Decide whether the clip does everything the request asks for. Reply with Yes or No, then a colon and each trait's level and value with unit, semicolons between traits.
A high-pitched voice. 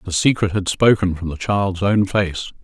No: very low, 95 Hz